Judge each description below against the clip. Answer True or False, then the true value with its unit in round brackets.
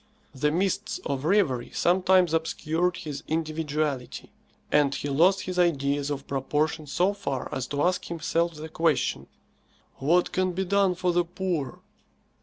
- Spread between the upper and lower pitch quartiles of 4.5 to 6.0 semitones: False (3.8 semitones)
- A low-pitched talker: False (160 Hz)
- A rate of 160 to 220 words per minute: False (145 wpm)